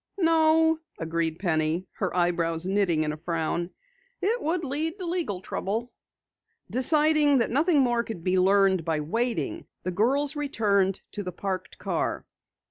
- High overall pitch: Yes, high, 205 Hz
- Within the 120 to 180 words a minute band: Yes, average, 145 wpm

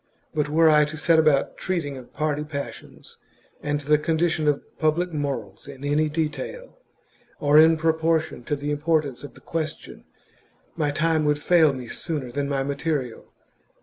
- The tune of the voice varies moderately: No, narrow, 2.0 semitones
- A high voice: No, medium, 150 Hz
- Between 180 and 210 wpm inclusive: No, average, 165 wpm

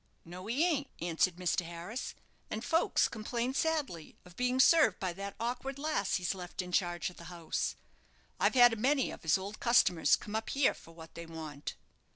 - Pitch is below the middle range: No, high, 200 Hz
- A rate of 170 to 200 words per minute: Yes, average, 190 wpm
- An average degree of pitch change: No, wide, 6.6 semitones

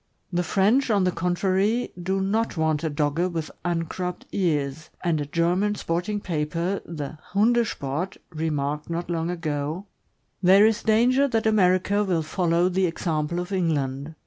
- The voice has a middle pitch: Yes, medium, 175 Hz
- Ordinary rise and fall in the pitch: Yes, average, 3.7 semitones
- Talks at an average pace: Yes, average, 150 wpm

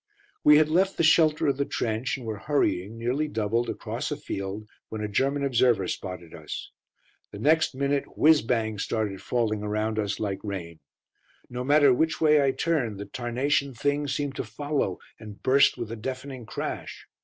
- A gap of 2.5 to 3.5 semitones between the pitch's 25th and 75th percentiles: No, average, 5.1 semitones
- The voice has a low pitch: Yes, low, 125 Hz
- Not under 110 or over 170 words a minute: No, average, 180 wpm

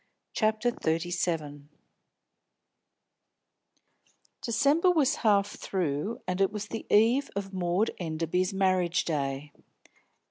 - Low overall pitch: No, medium, 185 Hz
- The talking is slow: Yes, slow, 100 wpm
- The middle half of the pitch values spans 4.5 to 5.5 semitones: Yes, average, 4.8 semitones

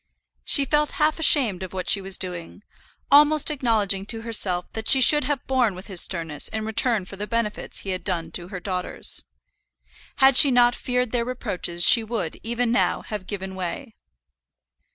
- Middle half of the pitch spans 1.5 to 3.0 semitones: No, average, 5.1 semitones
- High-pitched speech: Yes, high, 220 Hz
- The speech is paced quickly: No, average, 180 wpm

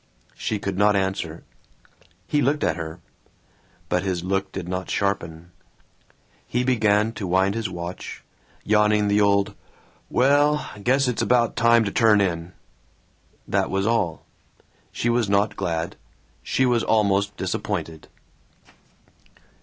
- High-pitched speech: No, low, 100 Hz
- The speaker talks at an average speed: No, slow, 130 wpm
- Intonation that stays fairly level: No, average, 3.7 semitones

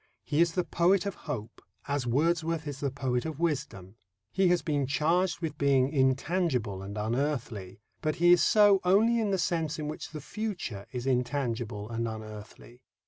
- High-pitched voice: No, medium, 145 Hz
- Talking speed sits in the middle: Yes, average, 175 wpm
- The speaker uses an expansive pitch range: Yes, wide, 6.0 semitones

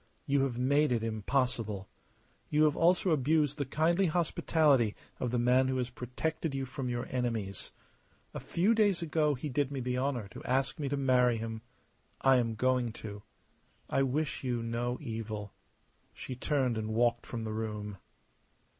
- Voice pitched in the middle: No, low, 125 Hz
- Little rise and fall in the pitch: No, average, 3.8 semitones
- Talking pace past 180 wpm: No, average, 170 wpm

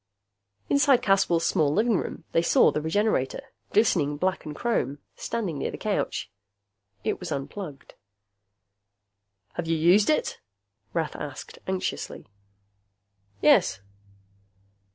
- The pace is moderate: No, slow, 110 wpm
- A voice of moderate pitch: Yes, medium, 175 Hz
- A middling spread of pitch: No, wide, 5.8 semitones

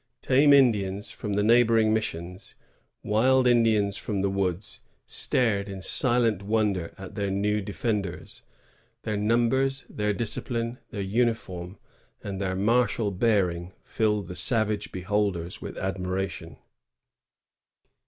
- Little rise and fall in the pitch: No, average, 3.2 semitones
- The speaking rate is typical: No, slow, 120 wpm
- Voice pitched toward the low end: Yes, low, 105 Hz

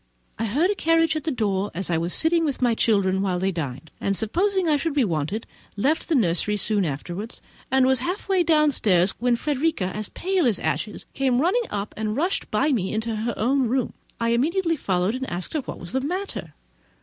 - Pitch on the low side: No, high, 235 Hz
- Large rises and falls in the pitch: Yes, wide, 7.7 semitones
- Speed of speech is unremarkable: No, fast, 210 wpm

